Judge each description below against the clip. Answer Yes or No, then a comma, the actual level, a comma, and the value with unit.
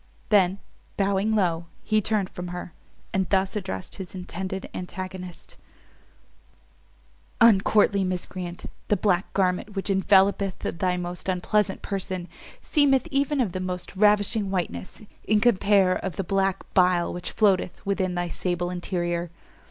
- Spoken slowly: Yes, slow, 130 wpm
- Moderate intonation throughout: No, narrow, 2.0 semitones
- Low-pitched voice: No, high, 190 Hz